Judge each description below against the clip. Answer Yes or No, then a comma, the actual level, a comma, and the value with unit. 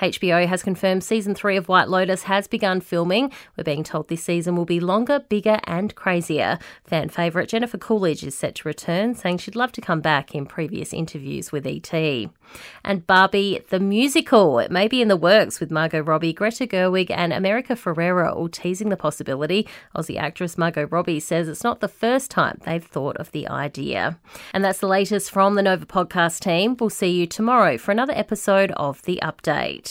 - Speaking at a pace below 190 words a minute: No, average, 195 wpm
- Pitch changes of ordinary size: Yes, average, 3.7 semitones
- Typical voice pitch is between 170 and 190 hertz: Yes, medium, 185 Hz